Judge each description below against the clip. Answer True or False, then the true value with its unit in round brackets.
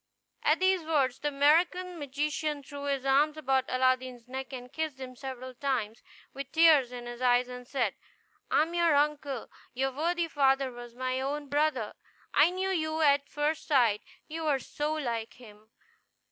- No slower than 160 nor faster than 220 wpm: True (170 wpm)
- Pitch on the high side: True (275 Hz)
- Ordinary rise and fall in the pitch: True (3.2 semitones)